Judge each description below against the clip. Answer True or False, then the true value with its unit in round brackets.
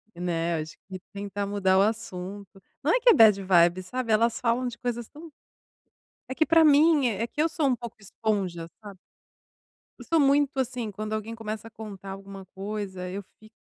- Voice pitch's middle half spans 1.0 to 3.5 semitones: False (4.2 semitones)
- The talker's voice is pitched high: True (215 Hz)